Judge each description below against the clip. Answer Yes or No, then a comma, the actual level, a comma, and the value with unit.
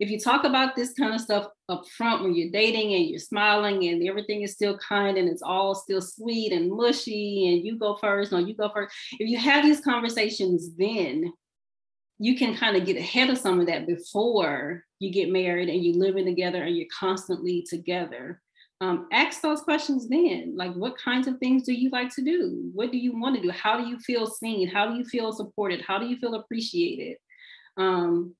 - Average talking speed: No, fast, 215 wpm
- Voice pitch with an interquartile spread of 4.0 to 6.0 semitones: Yes, average, 5.2 semitones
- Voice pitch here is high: Yes, high, 210 Hz